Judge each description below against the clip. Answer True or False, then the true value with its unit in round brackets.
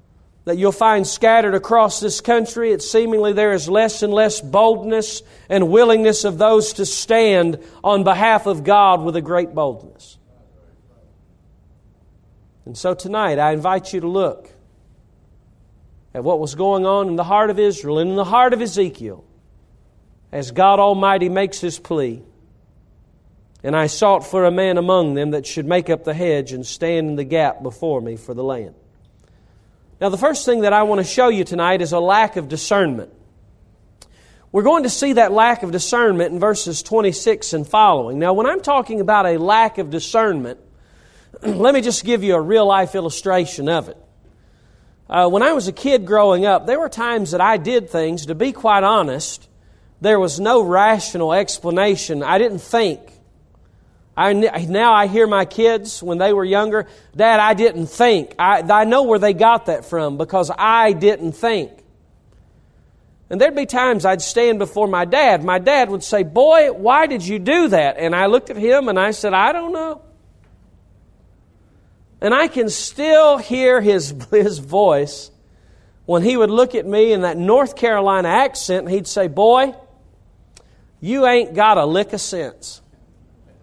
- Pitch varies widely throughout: True (6.7 semitones)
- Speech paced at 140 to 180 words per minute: True (175 wpm)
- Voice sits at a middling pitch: False (195 Hz)